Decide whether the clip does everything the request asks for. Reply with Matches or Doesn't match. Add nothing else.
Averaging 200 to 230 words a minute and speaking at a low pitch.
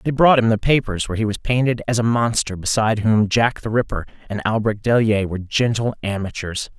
Matches